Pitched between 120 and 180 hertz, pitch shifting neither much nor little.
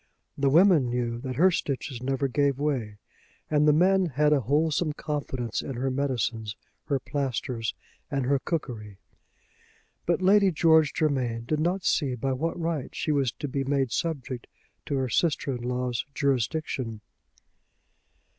Yes: medium, 140 Hz; average, 3.7 semitones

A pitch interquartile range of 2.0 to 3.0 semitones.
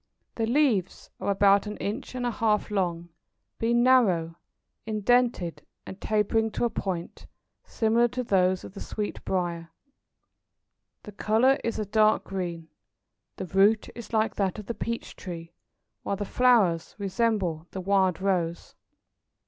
No: average, 3.7 semitones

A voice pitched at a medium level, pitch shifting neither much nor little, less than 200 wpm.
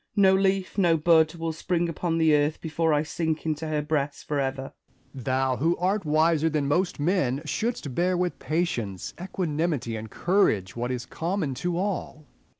Yes: medium, 160 Hz; average, 3.6 semitones; average, 175 wpm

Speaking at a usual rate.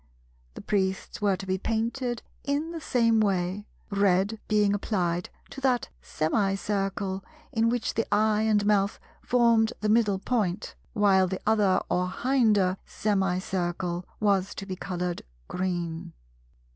No: slow, 130 wpm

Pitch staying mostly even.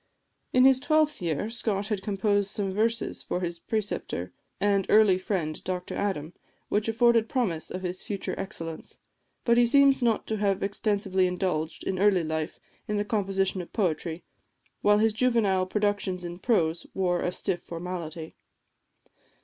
No: average, 3.3 semitones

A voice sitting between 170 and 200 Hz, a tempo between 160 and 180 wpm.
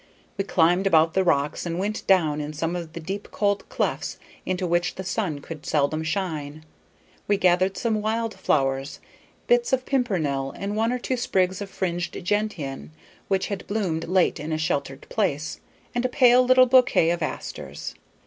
Yes: medium, 185 Hz; average, 175 wpm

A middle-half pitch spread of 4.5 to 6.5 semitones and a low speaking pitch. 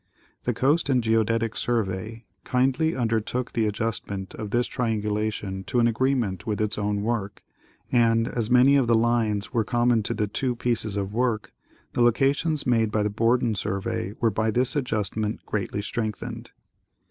No: narrow, 2.6 semitones; low, 115 Hz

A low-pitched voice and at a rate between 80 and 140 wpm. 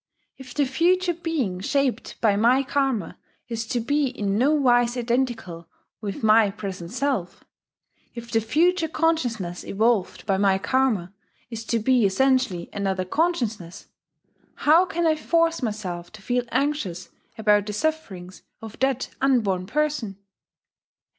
No: high, 235 Hz; slow, 135 wpm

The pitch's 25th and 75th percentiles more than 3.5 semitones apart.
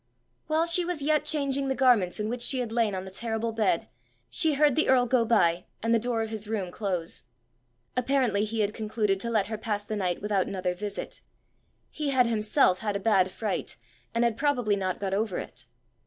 Yes: average, 3.9 semitones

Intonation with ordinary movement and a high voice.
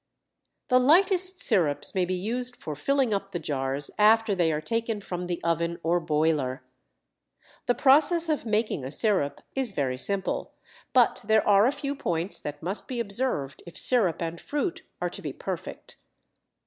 No: wide, 7.4 semitones; high, 200 Hz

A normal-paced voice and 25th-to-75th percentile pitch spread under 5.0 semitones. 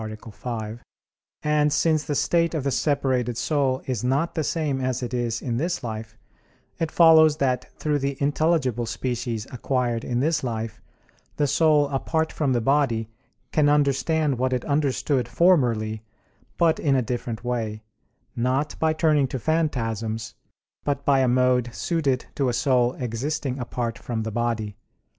Yes: average, 155 wpm; average, 3.9 semitones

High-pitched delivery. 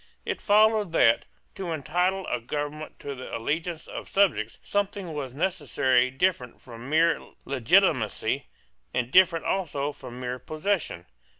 No: medium, 150 Hz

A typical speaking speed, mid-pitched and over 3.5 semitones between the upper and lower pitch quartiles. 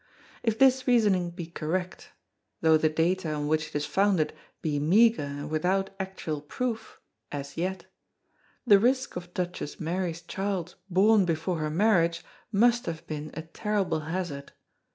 Yes: average, 150 wpm; medium, 175 Hz; average, 4.2 semitones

